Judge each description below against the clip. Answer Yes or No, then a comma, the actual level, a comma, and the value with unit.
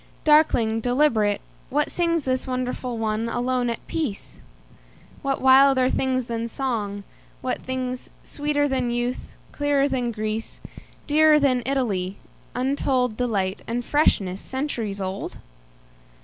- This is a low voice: No, very high, 250 Hz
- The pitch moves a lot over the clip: No, average, 3.4 semitones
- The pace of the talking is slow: Yes, slow, 100 wpm